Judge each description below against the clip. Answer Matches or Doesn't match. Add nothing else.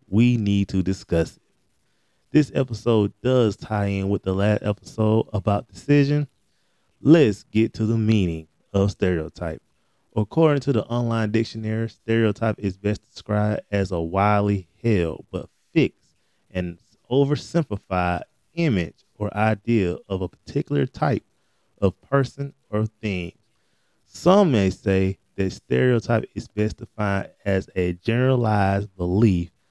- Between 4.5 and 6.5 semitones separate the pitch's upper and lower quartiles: Doesn't match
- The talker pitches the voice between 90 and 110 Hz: Matches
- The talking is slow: Matches